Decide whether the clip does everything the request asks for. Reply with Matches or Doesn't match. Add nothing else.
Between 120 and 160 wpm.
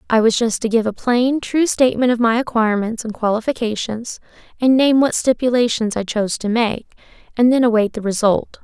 Doesn't match